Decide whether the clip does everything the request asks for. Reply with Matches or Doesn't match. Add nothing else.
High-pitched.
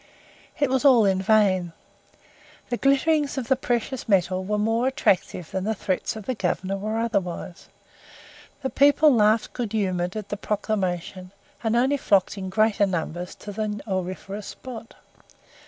Matches